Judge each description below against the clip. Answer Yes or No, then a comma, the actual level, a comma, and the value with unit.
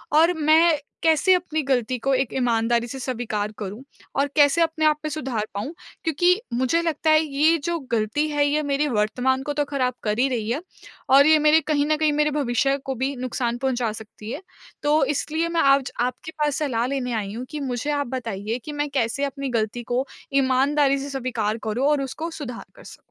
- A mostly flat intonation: No, average, 3.7 semitones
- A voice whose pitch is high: Yes, very high, 275 Hz